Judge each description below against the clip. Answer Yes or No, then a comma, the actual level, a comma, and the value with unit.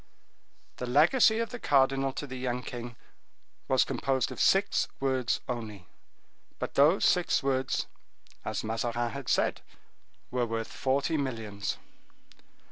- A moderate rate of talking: No, slow, 125 wpm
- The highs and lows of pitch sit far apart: No, average, 2.8 semitones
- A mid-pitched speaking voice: No, low, 130 Hz